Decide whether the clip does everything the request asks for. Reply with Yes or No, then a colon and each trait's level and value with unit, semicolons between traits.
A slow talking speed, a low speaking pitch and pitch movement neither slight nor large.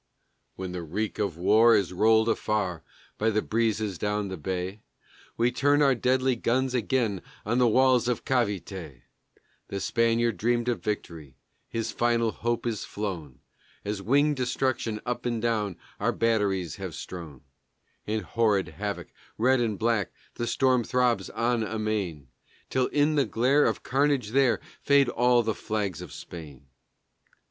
No: average, 150 wpm; low, 110 Hz; average, 3.9 semitones